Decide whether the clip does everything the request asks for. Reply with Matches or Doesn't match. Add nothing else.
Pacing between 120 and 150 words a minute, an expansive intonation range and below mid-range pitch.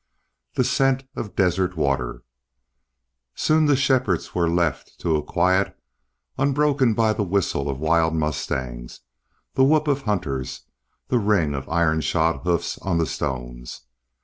Matches